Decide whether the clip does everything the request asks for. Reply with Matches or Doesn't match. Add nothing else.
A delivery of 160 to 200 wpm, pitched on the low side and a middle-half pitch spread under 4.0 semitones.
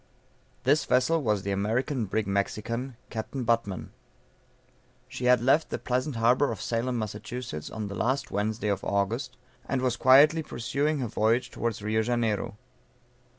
Doesn't match